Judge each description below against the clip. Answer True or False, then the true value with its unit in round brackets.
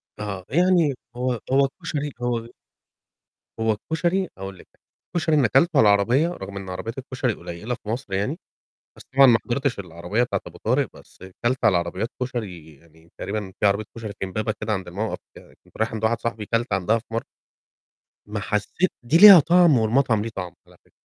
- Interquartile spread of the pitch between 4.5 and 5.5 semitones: True (5.2 semitones)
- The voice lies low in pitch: True (115 Hz)